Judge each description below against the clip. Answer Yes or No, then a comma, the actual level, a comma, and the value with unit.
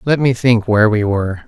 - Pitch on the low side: Yes, low, 115 Hz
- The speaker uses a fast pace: Yes, fast, 245 wpm